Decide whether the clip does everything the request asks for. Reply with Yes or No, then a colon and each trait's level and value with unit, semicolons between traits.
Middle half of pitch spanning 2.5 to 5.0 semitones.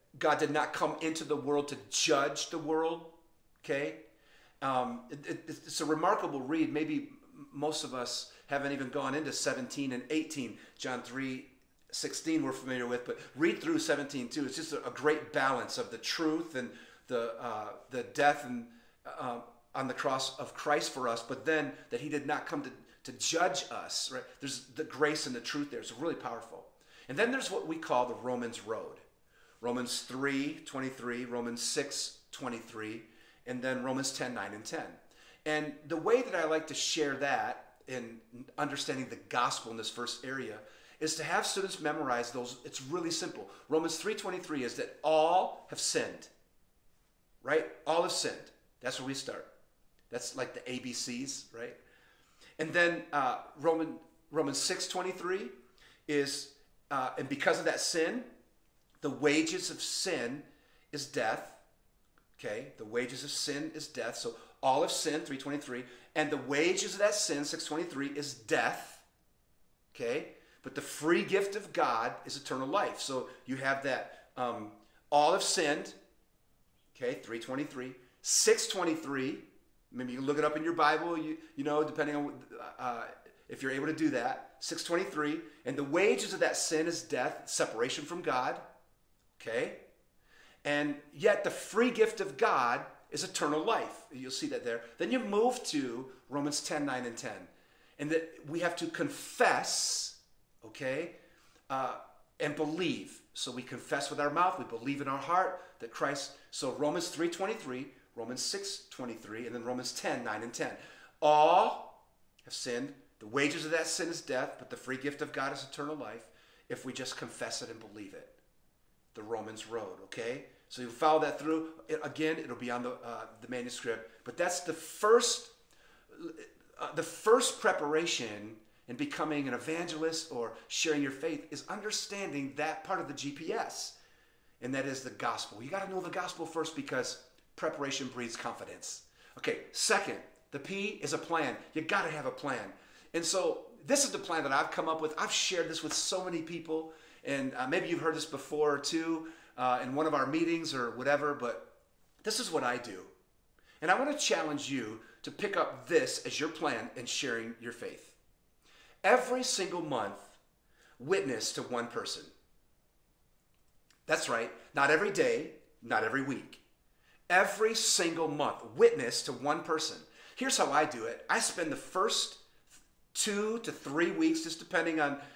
Yes: average, 4.2 semitones